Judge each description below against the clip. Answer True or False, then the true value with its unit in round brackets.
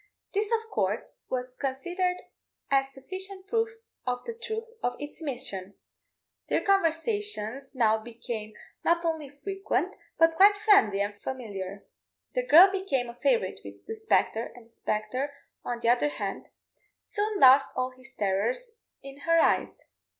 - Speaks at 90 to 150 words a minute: True (145 wpm)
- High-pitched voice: True (275 Hz)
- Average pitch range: False (8.5 semitones)